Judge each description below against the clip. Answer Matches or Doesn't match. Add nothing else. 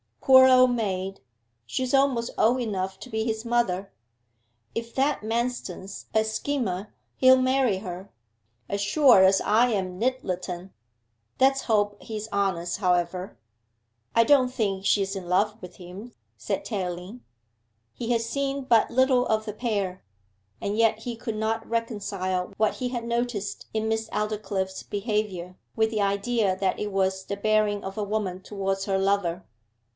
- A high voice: Matches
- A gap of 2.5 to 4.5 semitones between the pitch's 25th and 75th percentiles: Matches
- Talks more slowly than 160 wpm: Matches